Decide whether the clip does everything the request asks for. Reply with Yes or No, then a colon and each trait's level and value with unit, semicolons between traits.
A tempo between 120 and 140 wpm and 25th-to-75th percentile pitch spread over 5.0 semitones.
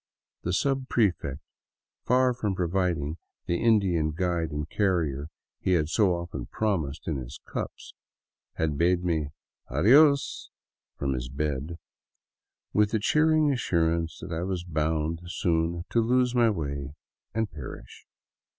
Yes: slow, 135 wpm; wide, 5.5 semitones